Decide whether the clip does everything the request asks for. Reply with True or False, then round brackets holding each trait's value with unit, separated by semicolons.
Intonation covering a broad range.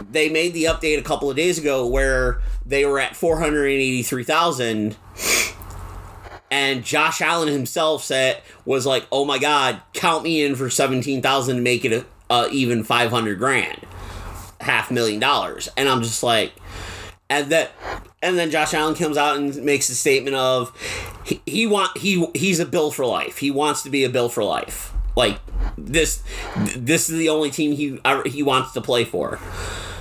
False (4.3 semitones)